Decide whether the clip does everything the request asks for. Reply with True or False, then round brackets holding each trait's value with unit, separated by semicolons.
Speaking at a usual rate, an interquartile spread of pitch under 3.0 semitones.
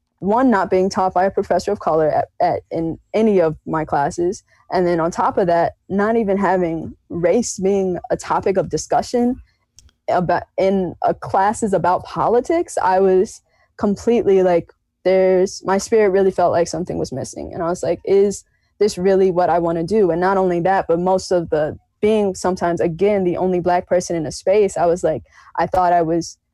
True (195 wpm; 2.5 semitones)